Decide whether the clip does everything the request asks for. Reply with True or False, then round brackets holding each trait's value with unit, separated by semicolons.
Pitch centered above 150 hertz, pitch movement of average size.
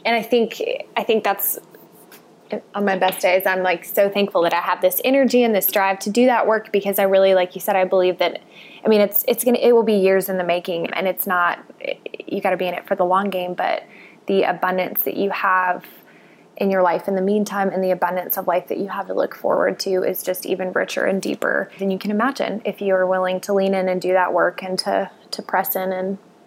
False (190 Hz; 2.0 semitones)